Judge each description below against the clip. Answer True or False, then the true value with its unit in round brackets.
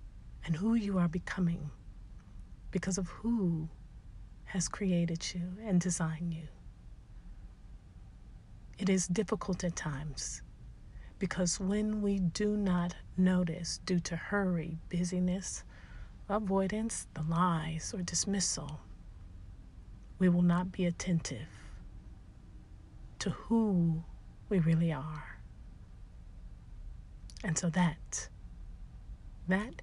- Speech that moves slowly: True (95 wpm)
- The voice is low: False (175 Hz)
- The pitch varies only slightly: False (4.1 semitones)